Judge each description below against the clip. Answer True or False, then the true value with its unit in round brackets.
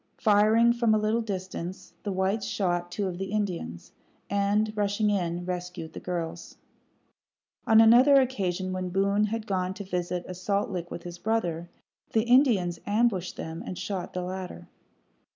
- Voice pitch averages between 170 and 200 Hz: True (190 Hz)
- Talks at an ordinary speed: True (160 wpm)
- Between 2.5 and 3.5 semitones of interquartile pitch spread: True (3.2 semitones)